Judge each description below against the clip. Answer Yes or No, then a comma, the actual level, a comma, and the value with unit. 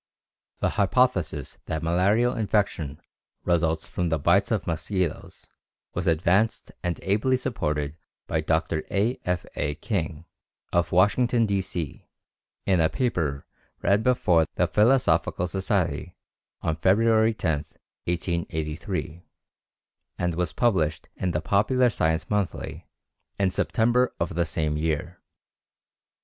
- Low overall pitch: Yes, very low, 90 Hz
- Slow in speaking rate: Yes, slow, 115 wpm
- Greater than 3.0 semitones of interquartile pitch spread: Yes, average, 4.8 semitones